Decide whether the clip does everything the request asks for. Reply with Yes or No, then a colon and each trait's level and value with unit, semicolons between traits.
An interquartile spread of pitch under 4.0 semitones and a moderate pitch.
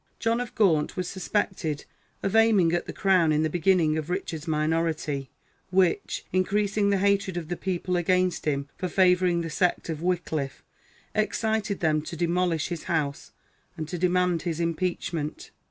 Yes: average, 2.9 semitones; medium, 175 Hz